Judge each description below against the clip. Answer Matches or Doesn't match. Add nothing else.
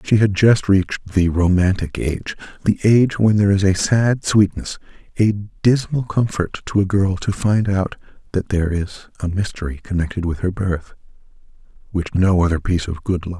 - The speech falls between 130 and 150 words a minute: Doesn't match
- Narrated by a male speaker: Matches